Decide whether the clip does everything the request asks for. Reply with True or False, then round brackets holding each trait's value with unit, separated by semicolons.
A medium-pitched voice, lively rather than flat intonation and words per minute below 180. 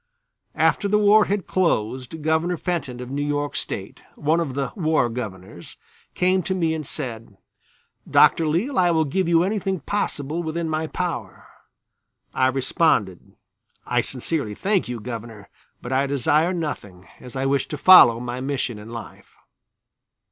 True (145 Hz; 5.7 semitones; 155 wpm)